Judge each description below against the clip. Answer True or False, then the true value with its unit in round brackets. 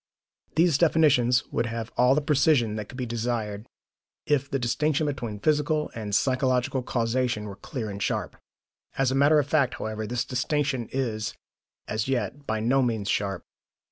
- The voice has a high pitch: False (125 Hz)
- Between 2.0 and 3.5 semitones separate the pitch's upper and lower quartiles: False (4.2 semitones)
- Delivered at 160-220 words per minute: True (165 wpm)